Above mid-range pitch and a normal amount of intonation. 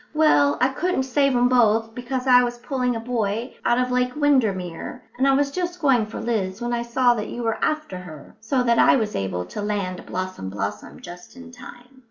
Yes: high, 240 Hz; average, 4.0 semitones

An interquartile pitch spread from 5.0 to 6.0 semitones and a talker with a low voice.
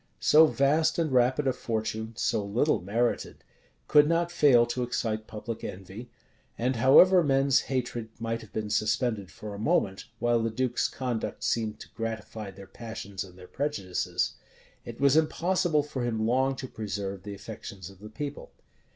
No: average, 4.0 semitones; low, 115 Hz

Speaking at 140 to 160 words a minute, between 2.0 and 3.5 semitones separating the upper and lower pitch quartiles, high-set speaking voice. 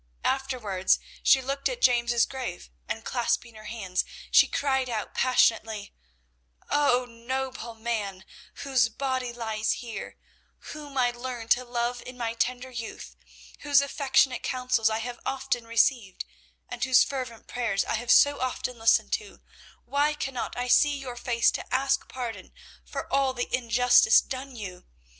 Yes: average, 150 wpm; narrow, 2.6 semitones; high, 245 Hz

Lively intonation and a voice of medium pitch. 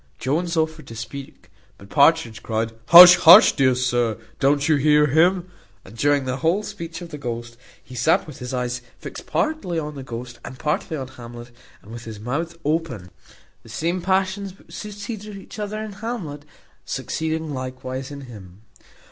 Yes: wide, 5.7 semitones; medium, 145 Hz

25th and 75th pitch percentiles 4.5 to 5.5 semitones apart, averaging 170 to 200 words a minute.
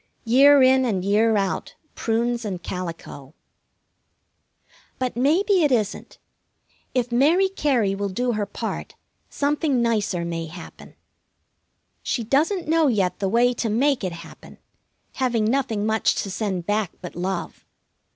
No: average, 5.2 semitones; slow, 135 wpm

